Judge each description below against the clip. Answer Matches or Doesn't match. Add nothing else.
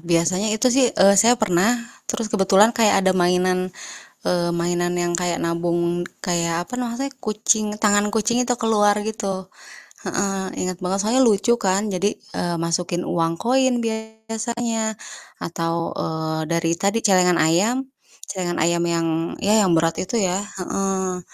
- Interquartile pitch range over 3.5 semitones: Matches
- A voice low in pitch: Doesn't match